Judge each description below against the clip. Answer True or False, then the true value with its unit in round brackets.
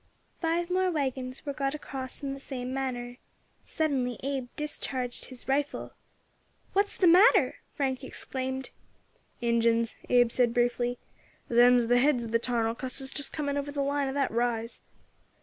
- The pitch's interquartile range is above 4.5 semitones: False (2.7 semitones)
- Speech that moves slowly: False (150 wpm)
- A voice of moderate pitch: False (260 Hz)